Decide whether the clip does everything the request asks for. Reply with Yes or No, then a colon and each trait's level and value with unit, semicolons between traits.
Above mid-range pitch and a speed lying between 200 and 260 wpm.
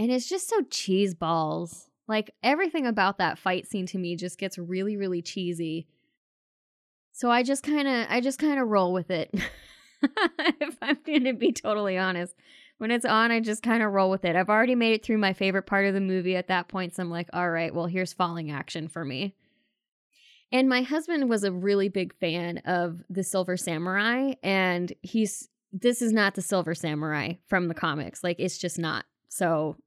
Yes: high, 195 Hz; fast, 205 wpm